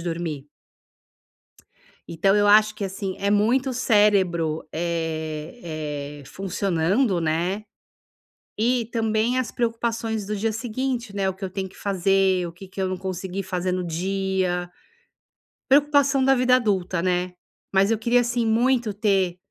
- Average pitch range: Yes, average, 4.1 semitones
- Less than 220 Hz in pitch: Yes, high, 195 Hz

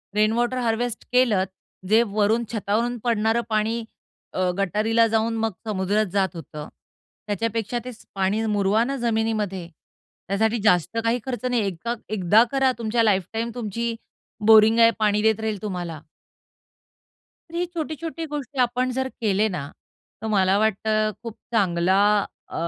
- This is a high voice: Yes, high, 220 Hz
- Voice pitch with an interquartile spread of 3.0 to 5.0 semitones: No, narrow, 2.5 semitones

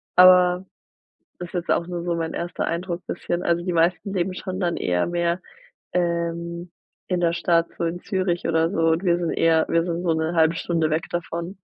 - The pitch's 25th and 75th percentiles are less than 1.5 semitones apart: Yes, narrow, 1.1 semitones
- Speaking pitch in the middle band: Yes, medium, 170 Hz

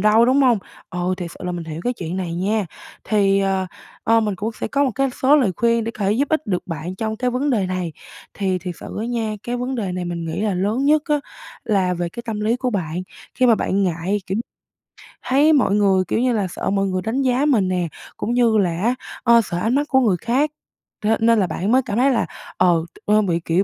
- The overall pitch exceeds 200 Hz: Yes, high, 210 Hz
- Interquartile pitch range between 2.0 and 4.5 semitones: No, average, 4.9 semitones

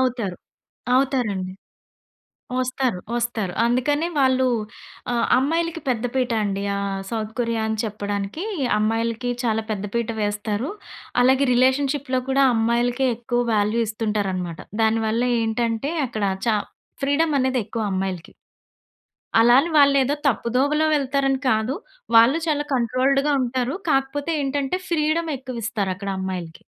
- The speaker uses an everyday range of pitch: Yes, average, 3.9 semitones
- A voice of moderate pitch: No, high, 240 Hz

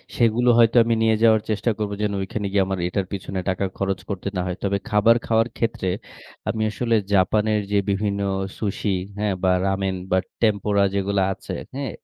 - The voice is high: No, low, 100 Hz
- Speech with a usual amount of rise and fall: No, narrow, 2.2 semitones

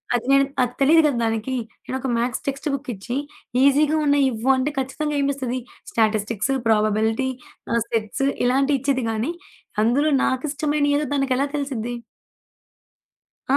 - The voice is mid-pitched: No, very high, 260 Hz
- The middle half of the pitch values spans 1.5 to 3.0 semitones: No, average, 3.4 semitones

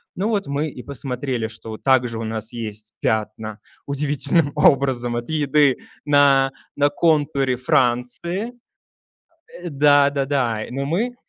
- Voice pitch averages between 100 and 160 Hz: Yes, low, 135 Hz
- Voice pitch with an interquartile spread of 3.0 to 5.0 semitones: Yes, average, 3.4 semitones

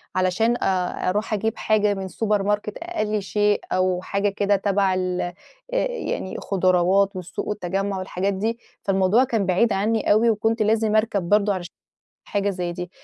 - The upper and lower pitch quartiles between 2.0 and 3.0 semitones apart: Yes, narrow, 2.4 semitones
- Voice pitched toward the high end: Yes, high, 200 Hz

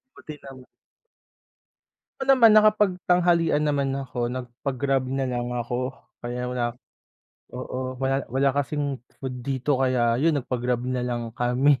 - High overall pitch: No, low, 130 Hz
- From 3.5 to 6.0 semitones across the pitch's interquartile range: No, narrow, 2.5 semitones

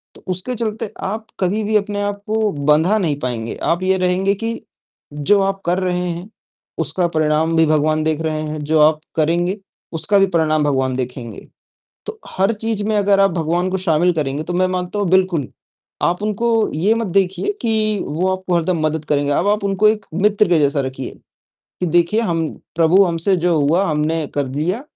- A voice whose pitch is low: No, medium, 175 Hz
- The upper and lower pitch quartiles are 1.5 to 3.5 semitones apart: No, average, 4.3 semitones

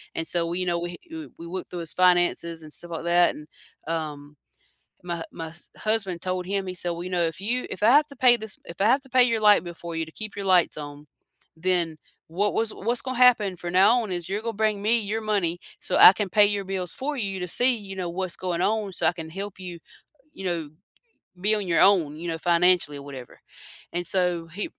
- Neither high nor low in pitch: Yes, medium, 180 Hz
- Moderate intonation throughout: Yes, average, 3.7 semitones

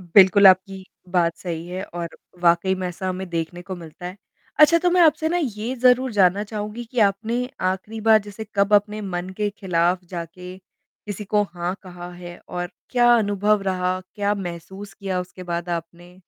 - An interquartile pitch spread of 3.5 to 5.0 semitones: No, average, 3.1 semitones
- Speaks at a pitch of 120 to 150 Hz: No, high, 190 Hz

